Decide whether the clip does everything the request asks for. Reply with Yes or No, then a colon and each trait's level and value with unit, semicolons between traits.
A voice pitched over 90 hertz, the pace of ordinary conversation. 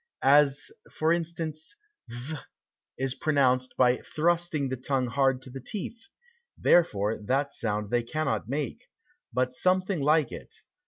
No: medium, 140 Hz; slow, 130 wpm